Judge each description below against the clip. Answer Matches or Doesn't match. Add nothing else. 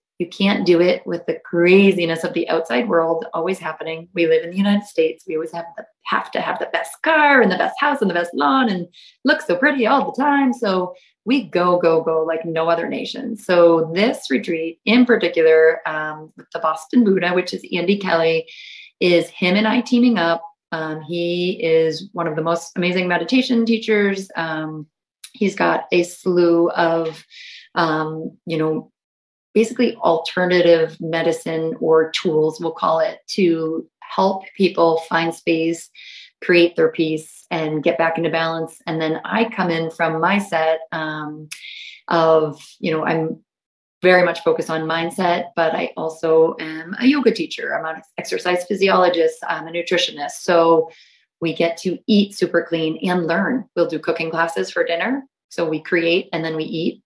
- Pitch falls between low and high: Matches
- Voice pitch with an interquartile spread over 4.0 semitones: Doesn't match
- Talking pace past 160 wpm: Matches